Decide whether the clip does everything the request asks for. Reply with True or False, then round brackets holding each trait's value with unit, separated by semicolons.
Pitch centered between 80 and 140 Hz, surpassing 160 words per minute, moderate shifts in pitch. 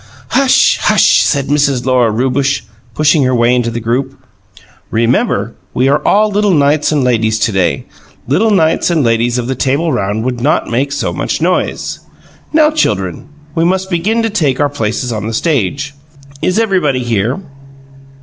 False (135 Hz; 170 wpm; 5.8 semitones)